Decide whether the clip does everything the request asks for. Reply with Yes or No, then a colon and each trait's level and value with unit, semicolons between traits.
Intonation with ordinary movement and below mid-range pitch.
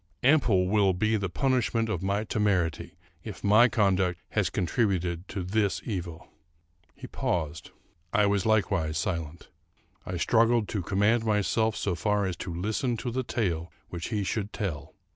Yes: average, 3.8 semitones; low, 100 Hz